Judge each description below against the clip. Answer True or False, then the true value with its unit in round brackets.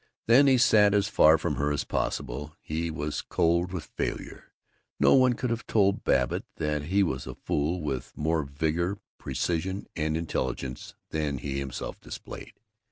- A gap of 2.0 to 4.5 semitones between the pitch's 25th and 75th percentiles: False (5.0 semitones)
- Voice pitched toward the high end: False (80 Hz)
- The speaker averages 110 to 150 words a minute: False (165 wpm)